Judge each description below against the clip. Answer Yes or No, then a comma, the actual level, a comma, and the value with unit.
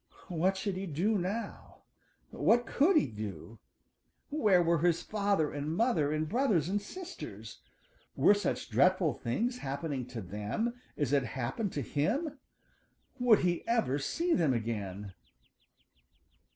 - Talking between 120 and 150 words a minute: Yes, slow, 135 wpm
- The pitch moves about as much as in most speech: No, wide, 8.2 semitones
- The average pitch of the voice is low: No, medium, 175 Hz